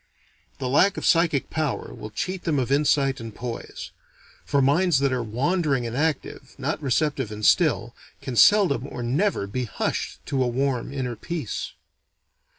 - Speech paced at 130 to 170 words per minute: Yes, average, 160 wpm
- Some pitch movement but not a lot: Yes, average, 4.1 semitones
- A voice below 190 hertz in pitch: Yes, low, 135 Hz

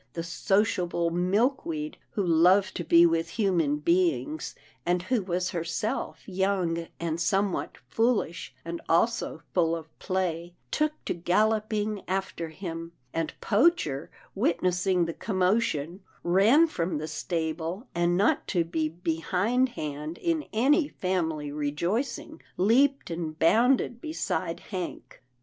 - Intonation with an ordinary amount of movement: Yes, average, 4.5 semitones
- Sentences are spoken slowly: Yes, slow, 120 wpm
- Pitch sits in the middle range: Yes, medium, 180 Hz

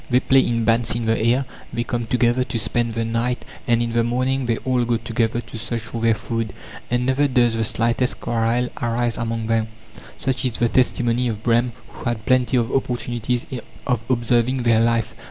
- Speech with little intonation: Yes, narrow, 1.4 semitones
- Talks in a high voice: No, low, 120 Hz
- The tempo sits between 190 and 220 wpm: Yes, average, 200 wpm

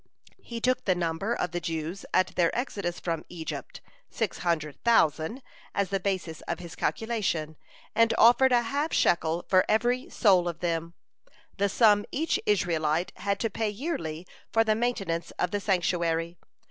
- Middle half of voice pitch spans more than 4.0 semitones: Yes, average, 5.1 semitones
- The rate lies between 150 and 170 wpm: Yes, average, 160 wpm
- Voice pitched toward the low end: No, medium, 185 Hz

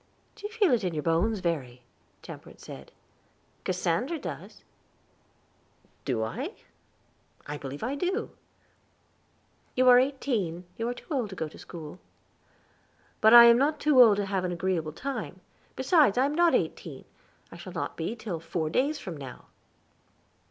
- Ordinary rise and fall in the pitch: No, wide, 8.1 semitones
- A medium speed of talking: Yes, average, 160 wpm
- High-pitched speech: Yes, high, 210 Hz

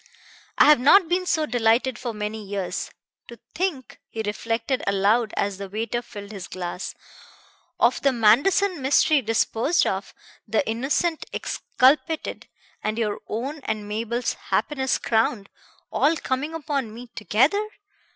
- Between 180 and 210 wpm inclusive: No, slow, 135 wpm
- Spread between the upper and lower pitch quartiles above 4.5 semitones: Yes, average, 5.1 semitones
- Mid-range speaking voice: No, high, 235 Hz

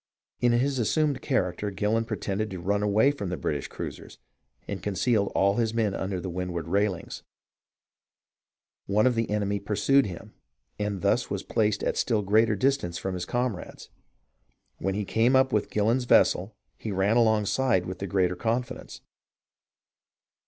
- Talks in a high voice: No, low, 105 Hz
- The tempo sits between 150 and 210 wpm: Yes, average, 160 wpm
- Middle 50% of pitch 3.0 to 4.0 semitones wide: Yes, average, 3.3 semitones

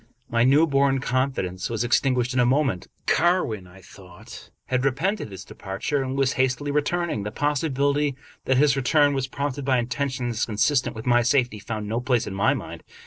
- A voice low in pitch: Yes, low, 130 Hz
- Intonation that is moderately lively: Yes, average, 3.6 semitones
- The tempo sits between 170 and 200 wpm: Yes, average, 180 wpm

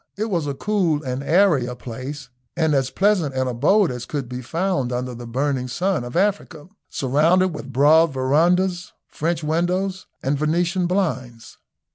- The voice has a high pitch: No, medium, 150 Hz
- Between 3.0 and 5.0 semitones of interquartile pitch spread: No, wide, 5.6 semitones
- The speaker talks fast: No, average, 160 wpm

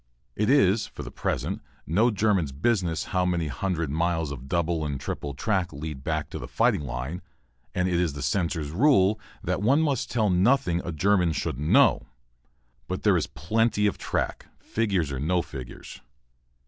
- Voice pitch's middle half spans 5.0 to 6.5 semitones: Yes, average, 5.3 semitones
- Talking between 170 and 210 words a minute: Yes, average, 175 wpm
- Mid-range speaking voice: No, very low, 85 Hz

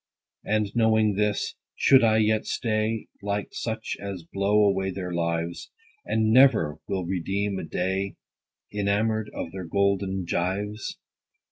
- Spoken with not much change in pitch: Yes, narrow, 2.3 semitones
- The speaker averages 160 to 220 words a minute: No, slow, 135 wpm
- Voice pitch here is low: Yes, low, 100 Hz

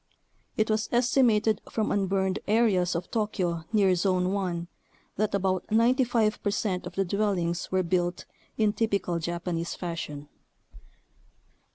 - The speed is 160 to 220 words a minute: No, slow, 135 wpm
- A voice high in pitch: Yes, high, 195 Hz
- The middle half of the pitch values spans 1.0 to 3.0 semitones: No, average, 3.5 semitones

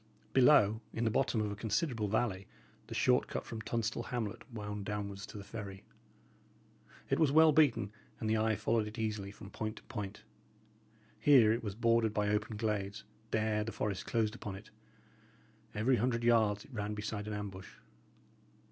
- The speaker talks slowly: No, average, 175 wpm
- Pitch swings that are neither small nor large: No, narrow, 2.0 semitones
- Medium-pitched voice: No, low, 110 Hz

